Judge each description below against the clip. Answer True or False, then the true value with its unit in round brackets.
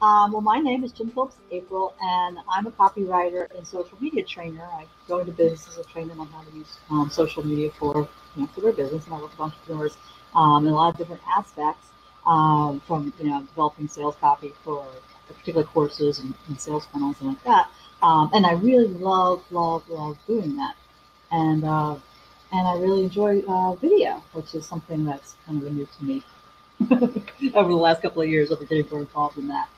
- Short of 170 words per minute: False (205 wpm)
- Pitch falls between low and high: True (165 Hz)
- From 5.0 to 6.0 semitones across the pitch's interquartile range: False (4.1 semitones)